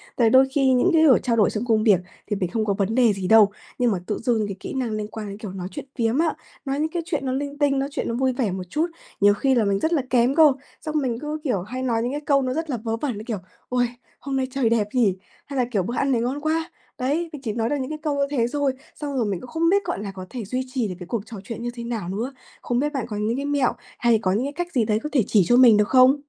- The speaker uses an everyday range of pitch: Yes, average, 4.4 semitones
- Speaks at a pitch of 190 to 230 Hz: No, high, 245 Hz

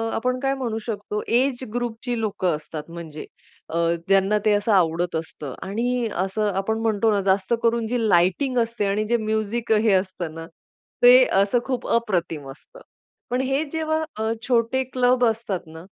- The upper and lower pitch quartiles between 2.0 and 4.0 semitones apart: No, average, 4.5 semitones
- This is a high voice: Yes, high, 220 Hz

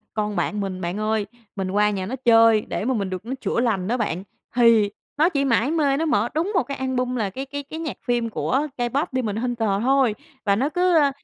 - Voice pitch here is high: Yes, high, 240 Hz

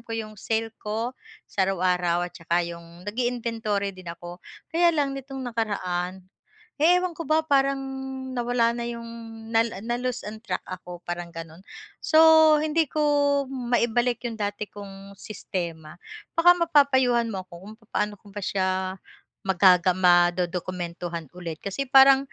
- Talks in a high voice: Yes, high, 210 Hz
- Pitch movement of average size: No, wide, 5.7 semitones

